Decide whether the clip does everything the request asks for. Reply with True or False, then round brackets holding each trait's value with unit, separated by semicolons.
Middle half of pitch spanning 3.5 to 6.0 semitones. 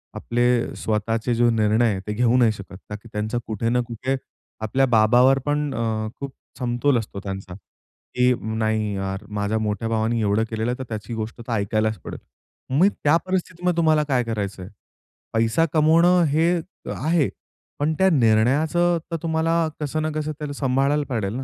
True (5.2 semitones)